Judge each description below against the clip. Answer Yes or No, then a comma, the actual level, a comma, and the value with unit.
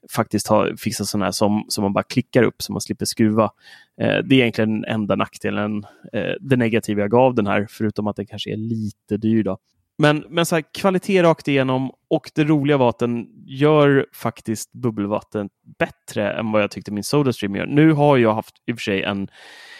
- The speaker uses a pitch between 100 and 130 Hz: Yes, low, 110 Hz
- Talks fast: Yes, fast, 210 wpm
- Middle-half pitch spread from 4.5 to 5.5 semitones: Yes, average, 4.9 semitones